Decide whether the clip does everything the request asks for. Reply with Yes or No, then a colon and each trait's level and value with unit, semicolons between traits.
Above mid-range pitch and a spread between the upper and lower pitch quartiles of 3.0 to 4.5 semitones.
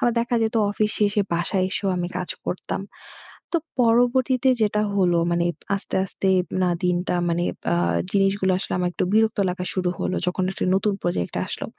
Yes: high, 195 Hz; average, 3.4 semitones